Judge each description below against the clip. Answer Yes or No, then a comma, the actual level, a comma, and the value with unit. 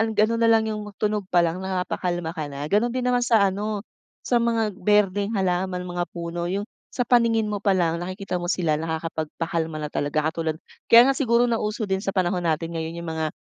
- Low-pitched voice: No, high, 190 Hz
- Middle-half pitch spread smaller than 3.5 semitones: No, average, 4.3 semitones